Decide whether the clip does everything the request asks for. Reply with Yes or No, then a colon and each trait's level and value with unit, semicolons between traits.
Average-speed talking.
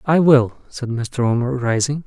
Yes: average, 175 wpm